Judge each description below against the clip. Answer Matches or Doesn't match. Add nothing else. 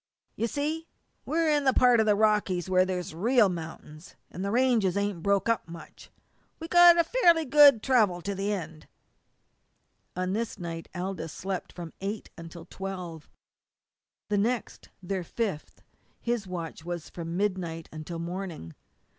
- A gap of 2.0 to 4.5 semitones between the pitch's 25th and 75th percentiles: Doesn't match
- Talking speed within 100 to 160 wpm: Matches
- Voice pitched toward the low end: Doesn't match